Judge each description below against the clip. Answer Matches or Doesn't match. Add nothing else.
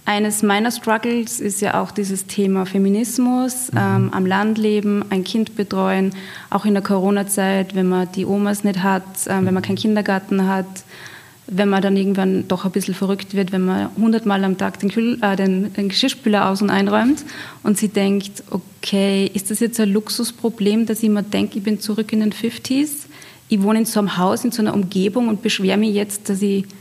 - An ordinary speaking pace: Doesn't match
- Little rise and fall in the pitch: Matches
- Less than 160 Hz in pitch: Doesn't match